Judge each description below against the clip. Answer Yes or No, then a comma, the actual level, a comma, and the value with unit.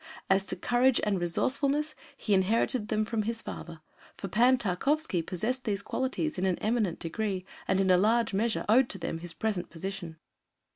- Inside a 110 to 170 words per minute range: No, average, 180 wpm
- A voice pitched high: Yes, high, 210 Hz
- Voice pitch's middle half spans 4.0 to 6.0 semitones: Yes, average, 4.5 semitones